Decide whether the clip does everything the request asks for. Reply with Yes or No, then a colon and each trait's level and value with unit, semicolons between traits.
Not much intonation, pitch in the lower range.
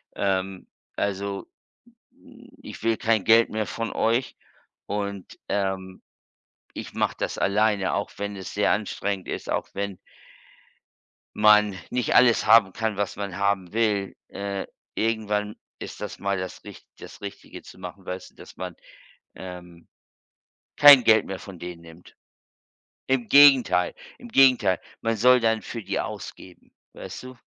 No: average, 3.0 semitones; low, 100 Hz